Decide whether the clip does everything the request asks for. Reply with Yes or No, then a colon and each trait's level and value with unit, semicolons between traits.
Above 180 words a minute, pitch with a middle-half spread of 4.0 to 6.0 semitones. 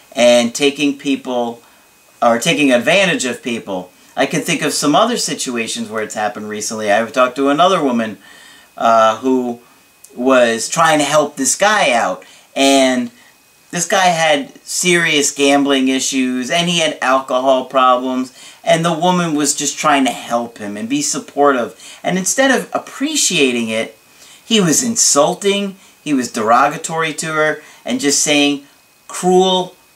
No: average, 150 wpm; average, 5.2 semitones